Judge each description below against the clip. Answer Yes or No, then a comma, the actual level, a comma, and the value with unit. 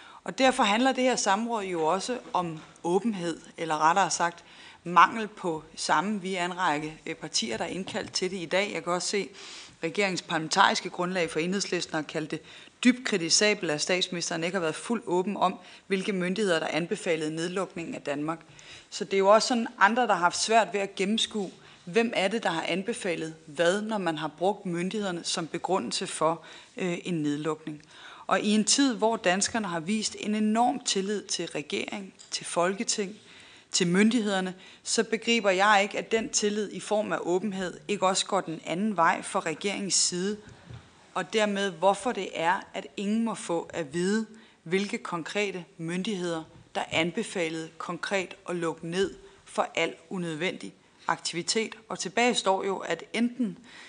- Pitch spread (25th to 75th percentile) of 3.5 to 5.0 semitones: Yes, average, 3.8 semitones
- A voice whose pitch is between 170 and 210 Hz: Yes, high, 190 Hz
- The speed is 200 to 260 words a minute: No, average, 175 wpm